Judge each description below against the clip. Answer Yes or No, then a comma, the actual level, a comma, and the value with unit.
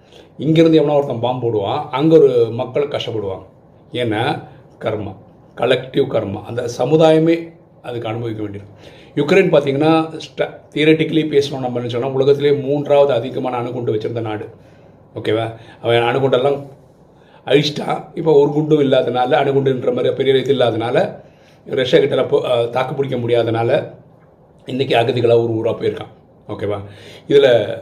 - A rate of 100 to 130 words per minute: Yes, average, 110 wpm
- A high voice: No, medium, 140 Hz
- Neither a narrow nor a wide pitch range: Yes, average, 4.8 semitones